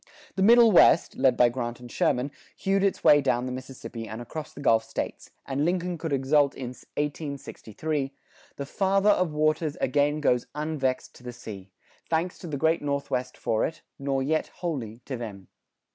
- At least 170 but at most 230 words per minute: Yes, average, 175 wpm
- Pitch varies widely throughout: No, average, 4.2 semitones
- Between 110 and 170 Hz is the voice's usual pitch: Yes, medium, 140 Hz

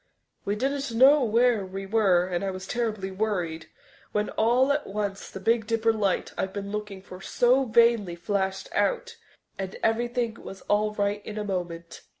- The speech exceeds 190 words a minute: No, average, 170 wpm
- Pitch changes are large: No, average, 3.4 semitones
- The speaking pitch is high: Yes, high, 210 Hz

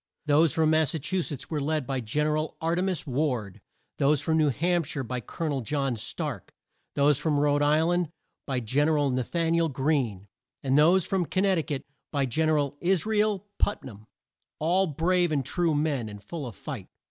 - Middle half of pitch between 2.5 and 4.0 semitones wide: Yes, average, 3.6 semitones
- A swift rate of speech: Yes, fast, 230 wpm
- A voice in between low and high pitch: Yes, medium, 150 Hz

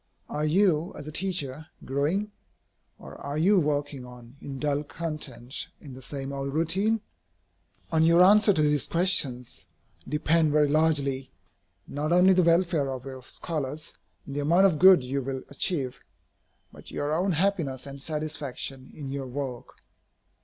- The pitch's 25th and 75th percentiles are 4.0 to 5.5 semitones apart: No, average, 3.6 semitones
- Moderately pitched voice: Yes, medium, 150 Hz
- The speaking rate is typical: Yes, average, 155 wpm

